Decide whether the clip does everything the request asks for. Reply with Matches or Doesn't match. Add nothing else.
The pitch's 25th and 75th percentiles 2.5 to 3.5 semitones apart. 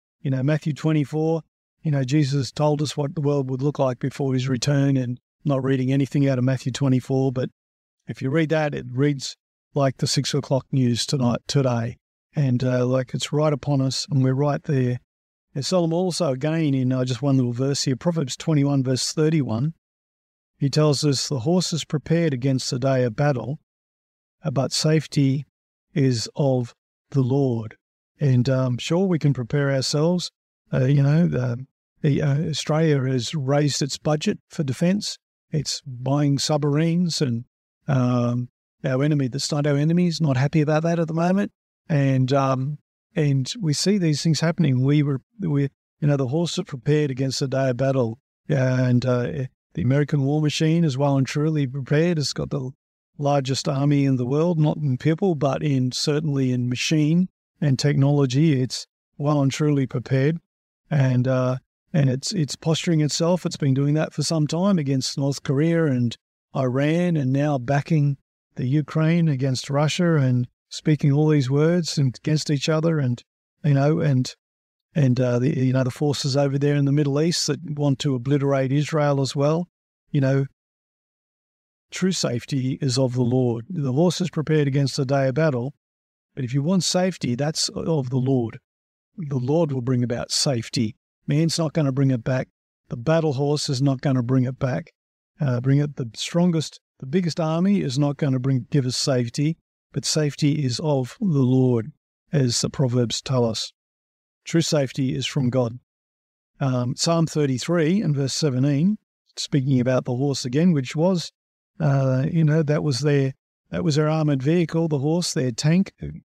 Matches